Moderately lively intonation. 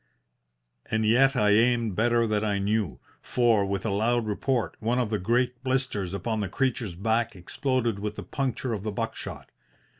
Yes: average, 3.0 semitones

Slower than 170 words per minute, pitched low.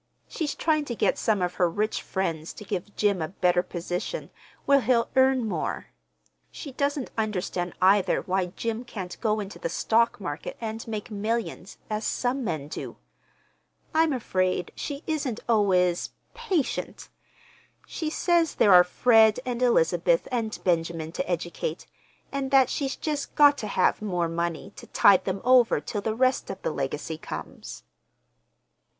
No: average, 155 wpm; high, 215 Hz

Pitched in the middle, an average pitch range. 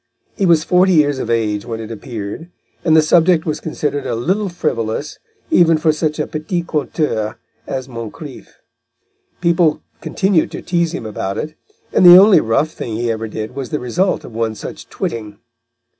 No: medium, 150 Hz; wide, 6.9 semitones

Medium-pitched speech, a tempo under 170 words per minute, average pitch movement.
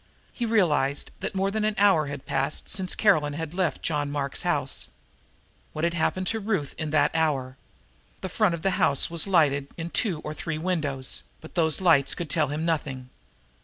No: medium, 160 Hz; average, 190 wpm; average, 4.3 semitones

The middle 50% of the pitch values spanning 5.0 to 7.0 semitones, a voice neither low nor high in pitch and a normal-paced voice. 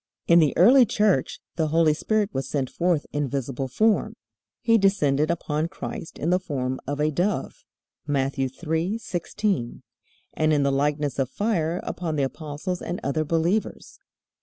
No: average, 4.4 semitones; medium, 155 Hz; average, 155 wpm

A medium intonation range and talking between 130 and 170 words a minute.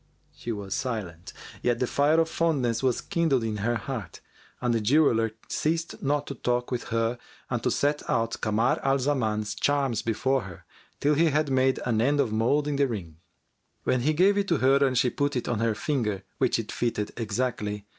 No: average, 4.2 semitones; average, 195 wpm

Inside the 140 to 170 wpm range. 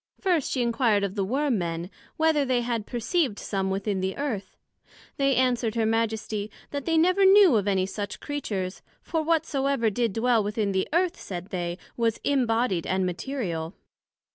Yes: average, 165 wpm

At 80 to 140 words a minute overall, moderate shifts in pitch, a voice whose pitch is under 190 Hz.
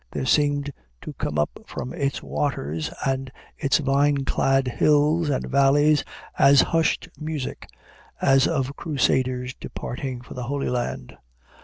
No: slow, 135 wpm; narrow, 2.2 semitones; low, 135 Hz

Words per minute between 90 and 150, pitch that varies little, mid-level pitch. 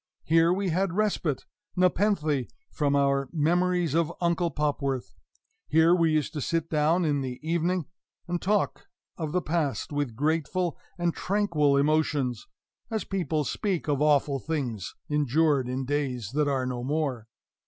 No: average, 145 wpm; average, 3.6 semitones; medium, 155 Hz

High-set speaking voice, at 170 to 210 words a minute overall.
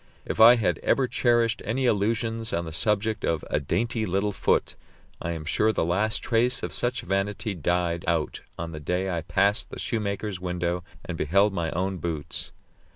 No: low, 100 Hz; average, 180 wpm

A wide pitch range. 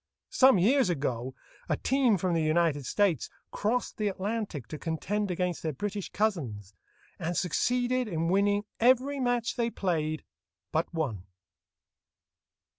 Yes: wide, 6.2 semitones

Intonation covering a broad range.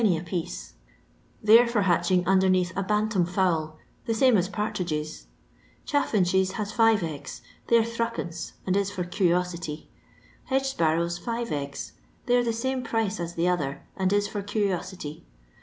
No: average, 4.2 semitones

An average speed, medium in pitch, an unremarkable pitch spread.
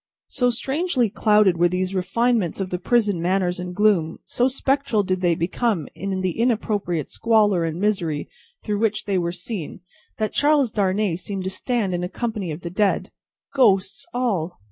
No: average, 170 wpm; high, 195 Hz; average, 4.2 semitones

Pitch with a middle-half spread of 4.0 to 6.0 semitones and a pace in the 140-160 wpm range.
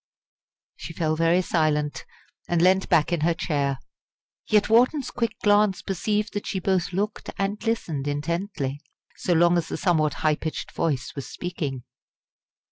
Yes: average, 4.6 semitones; average, 150 wpm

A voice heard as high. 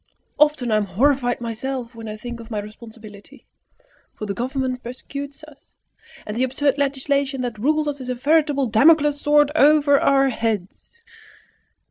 Yes: very high, 260 Hz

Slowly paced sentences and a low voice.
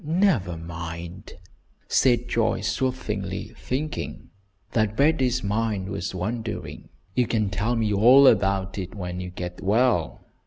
Yes: slow, 125 wpm; low, 105 Hz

